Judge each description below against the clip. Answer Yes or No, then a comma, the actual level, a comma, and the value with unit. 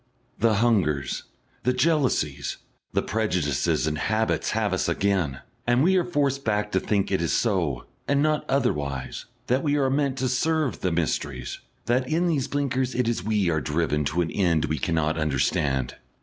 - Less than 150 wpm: No, average, 180 wpm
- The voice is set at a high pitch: No, low, 105 Hz